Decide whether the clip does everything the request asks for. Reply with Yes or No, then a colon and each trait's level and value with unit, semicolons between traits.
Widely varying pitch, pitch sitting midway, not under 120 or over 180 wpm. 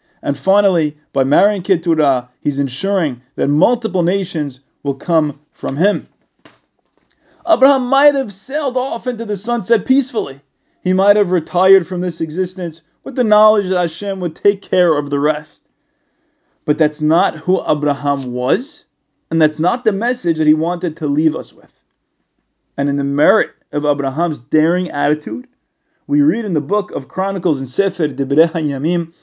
Yes: wide, 5.9 semitones; medium, 175 Hz; average, 160 wpm